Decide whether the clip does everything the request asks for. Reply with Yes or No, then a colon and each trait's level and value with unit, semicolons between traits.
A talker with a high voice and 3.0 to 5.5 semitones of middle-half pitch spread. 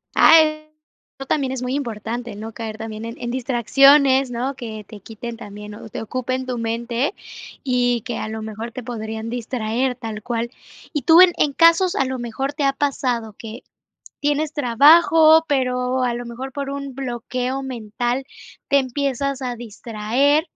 Yes: very high, 250 Hz; average, 3.3 semitones